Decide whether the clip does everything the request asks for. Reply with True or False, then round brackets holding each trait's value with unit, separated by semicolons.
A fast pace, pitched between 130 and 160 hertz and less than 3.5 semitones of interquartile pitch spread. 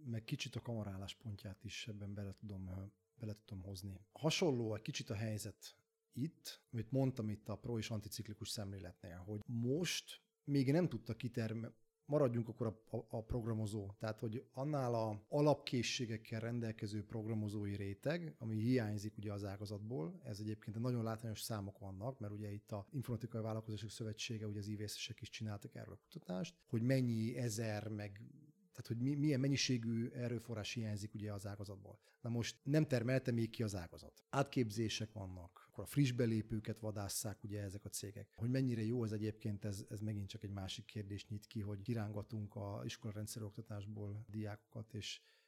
False (165 wpm; 110 Hz; 2.8 semitones)